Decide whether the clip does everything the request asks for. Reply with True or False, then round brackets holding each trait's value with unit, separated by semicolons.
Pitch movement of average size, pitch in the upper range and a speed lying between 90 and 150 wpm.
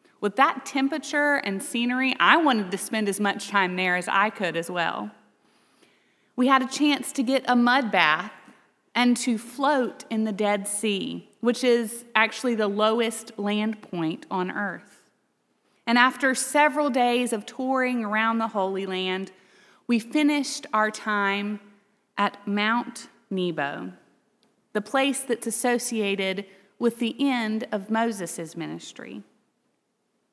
True (3.8 semitones; 225 Hz; 140 wpm)